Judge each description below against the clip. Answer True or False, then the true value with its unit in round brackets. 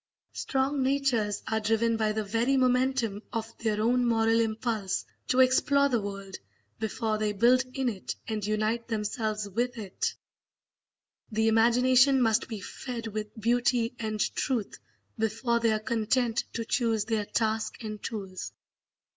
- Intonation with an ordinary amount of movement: False (2.3 semitones)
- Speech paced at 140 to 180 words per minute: True (145 wpm)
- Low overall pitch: False (225 Hz)